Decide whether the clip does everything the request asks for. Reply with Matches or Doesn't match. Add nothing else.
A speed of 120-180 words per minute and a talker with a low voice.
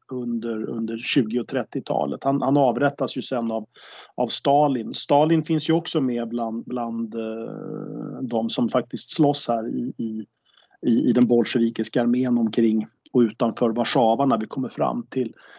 Matches